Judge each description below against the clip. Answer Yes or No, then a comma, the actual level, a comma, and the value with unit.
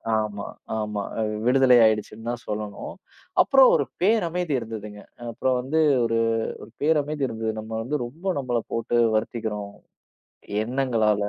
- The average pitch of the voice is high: No, low, 115 Hz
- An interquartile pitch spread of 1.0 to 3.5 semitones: No, average, 4.2 semitones